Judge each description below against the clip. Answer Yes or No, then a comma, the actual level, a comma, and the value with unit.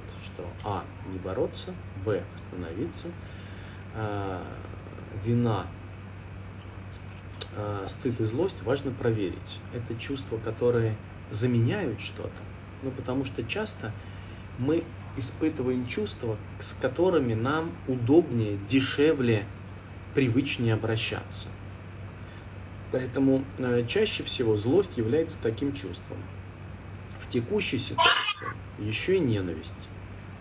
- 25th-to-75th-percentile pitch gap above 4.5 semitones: No, average, 3.6 semitones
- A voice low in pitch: Yes, low, 105 Hz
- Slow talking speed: Yes, slow, 95 wpm